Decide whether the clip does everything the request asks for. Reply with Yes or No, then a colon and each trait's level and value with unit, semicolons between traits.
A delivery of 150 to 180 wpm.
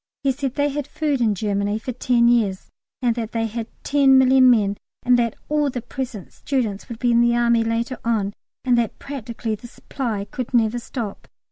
No: average, 200 wpm